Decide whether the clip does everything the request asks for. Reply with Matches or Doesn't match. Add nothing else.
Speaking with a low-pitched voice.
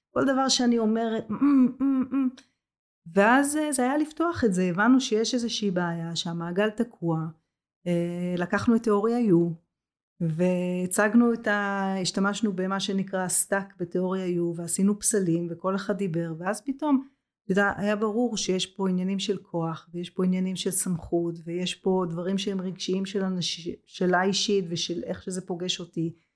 Doesn't match